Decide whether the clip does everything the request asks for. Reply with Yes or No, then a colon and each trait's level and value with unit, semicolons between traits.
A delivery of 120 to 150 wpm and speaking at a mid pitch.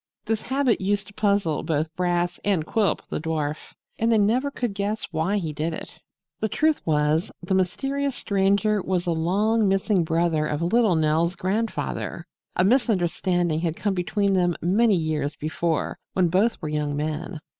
No: average, 165 wpm; medium, 180 Hz